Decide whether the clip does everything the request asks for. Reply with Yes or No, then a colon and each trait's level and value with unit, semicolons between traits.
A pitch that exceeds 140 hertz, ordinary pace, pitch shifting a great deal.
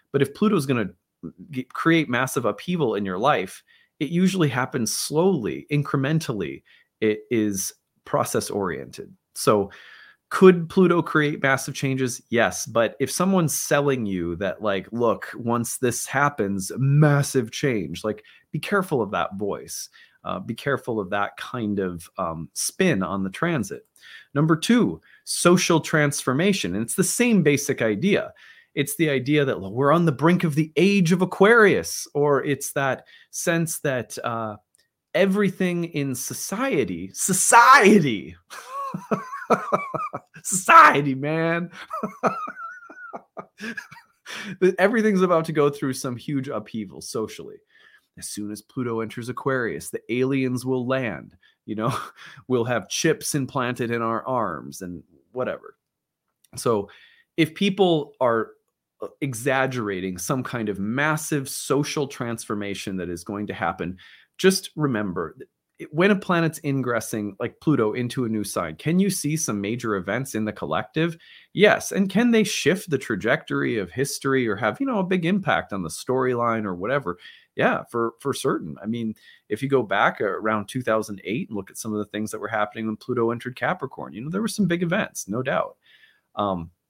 No: low, 135 Hz; average, 150 wpm; wide, 7.5 semitones